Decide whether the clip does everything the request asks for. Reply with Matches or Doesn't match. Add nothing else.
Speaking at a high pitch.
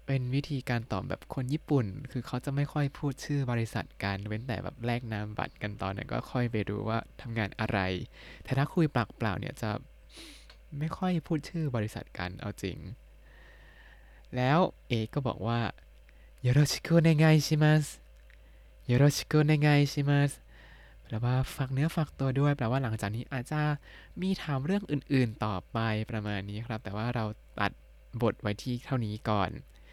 Doesn't match